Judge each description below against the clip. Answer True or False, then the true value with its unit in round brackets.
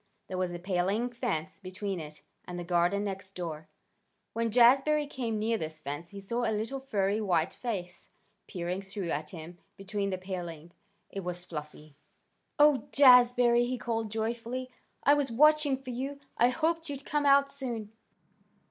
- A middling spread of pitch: False (6.0 semitones)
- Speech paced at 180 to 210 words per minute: False (165 wpm)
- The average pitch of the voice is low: False (210 Hz)